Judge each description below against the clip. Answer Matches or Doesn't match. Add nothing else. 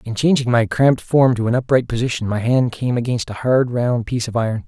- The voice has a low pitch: Matches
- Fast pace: Matches